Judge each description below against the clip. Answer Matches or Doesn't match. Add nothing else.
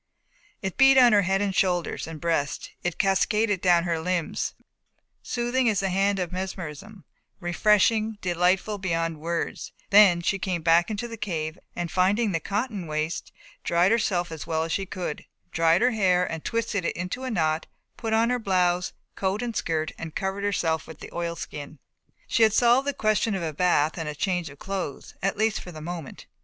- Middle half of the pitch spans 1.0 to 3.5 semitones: Doesn't match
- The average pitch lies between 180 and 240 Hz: Matches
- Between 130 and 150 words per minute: Doesn't match